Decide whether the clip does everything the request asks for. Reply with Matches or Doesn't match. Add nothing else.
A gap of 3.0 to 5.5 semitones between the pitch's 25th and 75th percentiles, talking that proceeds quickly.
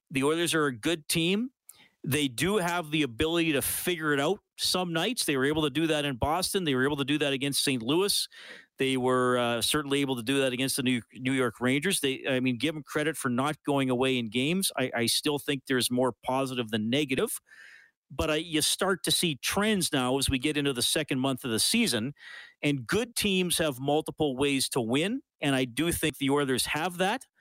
Matches